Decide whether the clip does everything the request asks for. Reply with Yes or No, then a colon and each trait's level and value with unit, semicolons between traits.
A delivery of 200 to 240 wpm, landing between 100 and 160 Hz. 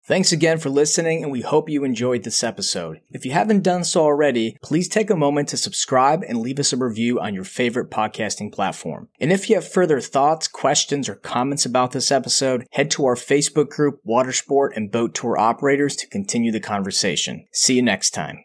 Yes: fast, 205 wpm; medium, 140 Hz